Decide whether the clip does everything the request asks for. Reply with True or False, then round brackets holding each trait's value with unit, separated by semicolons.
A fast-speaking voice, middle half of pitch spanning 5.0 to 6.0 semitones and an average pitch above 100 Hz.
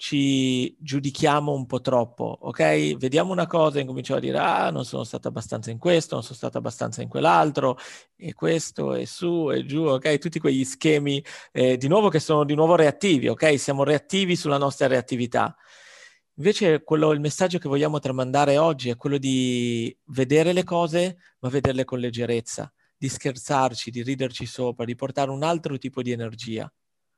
False (175 wpm; 3.6 semitones; 140 Hz)